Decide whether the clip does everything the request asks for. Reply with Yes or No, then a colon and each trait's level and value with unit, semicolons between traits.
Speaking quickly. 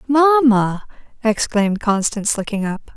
No: slow, 100 wpm